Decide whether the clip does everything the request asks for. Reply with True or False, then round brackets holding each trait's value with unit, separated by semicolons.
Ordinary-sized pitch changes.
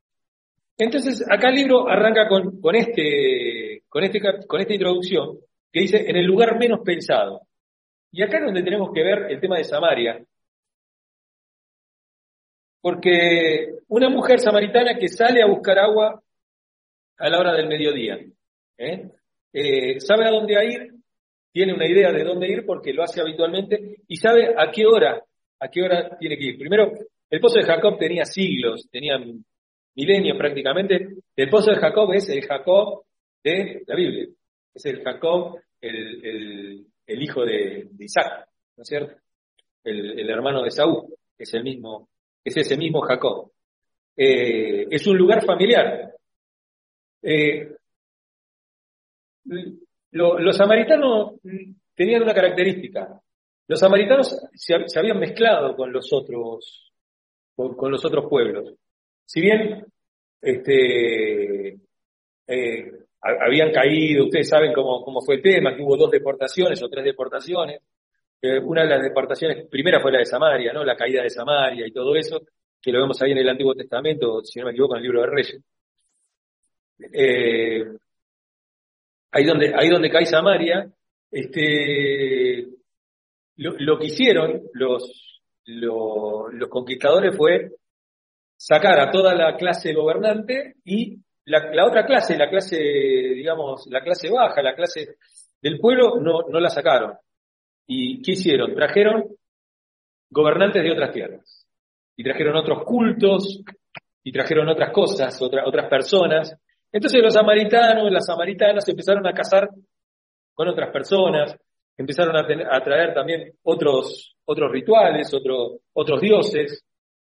False (7.3 semitones)